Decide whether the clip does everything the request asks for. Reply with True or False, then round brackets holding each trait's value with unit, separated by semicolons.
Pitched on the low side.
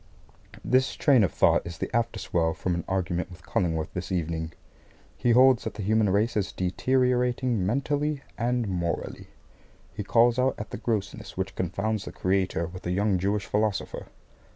True (105 Hz)